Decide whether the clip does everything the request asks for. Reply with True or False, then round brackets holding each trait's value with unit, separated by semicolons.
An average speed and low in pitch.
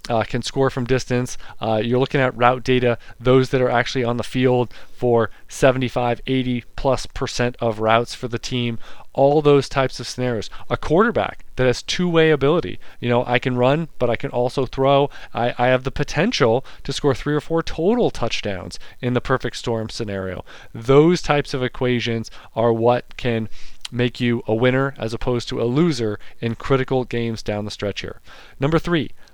True (190 wpm; 125 Hz)